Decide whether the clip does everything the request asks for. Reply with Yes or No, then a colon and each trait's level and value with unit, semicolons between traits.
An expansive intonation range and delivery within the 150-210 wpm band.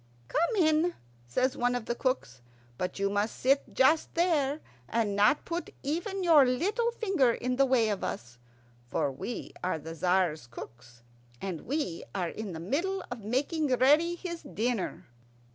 Yes: wide, 8.7 semitones; average, 160 wpm